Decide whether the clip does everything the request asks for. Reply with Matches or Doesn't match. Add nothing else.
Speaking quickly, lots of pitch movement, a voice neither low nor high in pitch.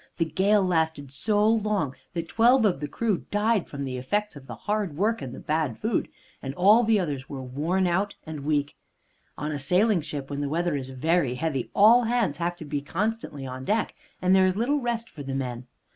Matches